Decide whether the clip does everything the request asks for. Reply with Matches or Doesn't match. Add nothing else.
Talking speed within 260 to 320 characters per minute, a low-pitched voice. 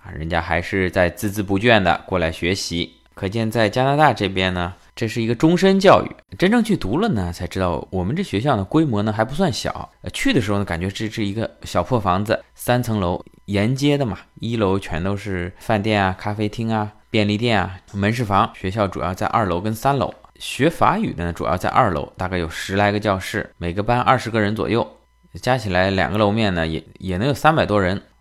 Matches